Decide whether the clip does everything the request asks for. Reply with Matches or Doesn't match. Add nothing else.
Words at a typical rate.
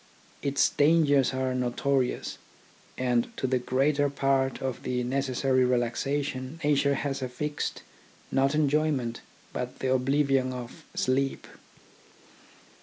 Doesn't match